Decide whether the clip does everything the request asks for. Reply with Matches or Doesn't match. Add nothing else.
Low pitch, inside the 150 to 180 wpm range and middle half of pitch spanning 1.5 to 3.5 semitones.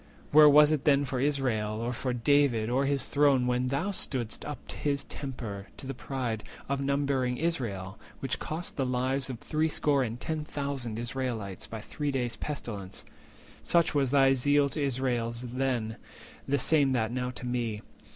Matches